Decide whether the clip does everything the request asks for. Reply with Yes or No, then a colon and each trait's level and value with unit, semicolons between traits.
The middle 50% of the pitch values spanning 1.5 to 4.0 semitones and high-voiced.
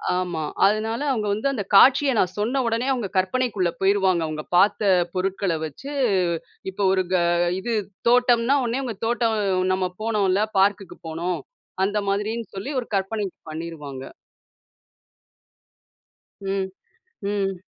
Yes: average, 3.7 semitones; high, 200 Hz